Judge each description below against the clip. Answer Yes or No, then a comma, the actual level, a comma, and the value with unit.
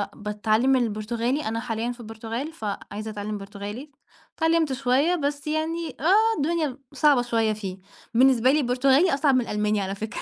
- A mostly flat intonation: No, average, 5.2 semitones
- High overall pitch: Yes, high, 245 Hz